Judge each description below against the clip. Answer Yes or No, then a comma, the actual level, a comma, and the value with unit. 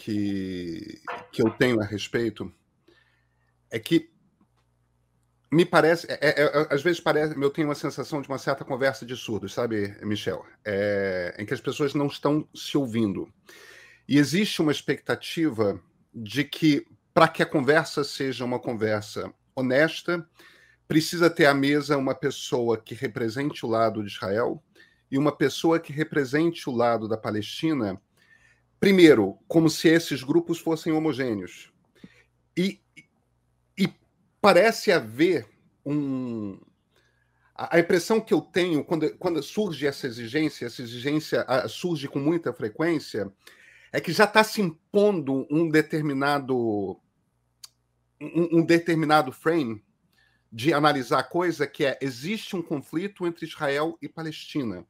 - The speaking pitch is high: No, medium, 145 Hz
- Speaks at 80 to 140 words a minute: Yes, average, 135 wpm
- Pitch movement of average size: No, wide, 6.3 semitones